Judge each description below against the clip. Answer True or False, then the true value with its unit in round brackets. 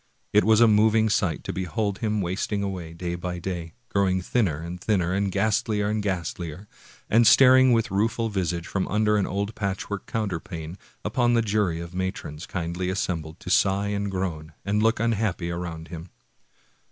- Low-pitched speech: True (95 Hz)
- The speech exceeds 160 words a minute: True (170 wpm)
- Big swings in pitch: False (3.4 semitones)